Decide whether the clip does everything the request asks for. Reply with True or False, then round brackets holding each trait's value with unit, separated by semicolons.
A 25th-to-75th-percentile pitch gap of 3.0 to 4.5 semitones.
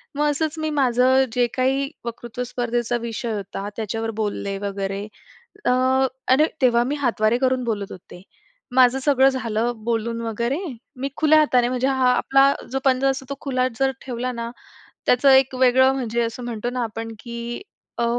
False (2.4 semitones)